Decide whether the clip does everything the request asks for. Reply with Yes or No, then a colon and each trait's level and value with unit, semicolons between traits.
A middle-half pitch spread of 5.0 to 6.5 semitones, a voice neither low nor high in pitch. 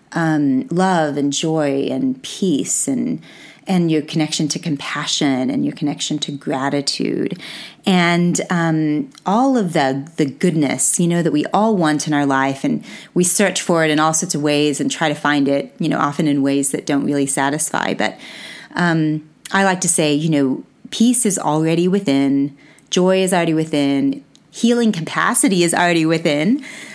No: average, 3.7 semitones; medium, 155 Hz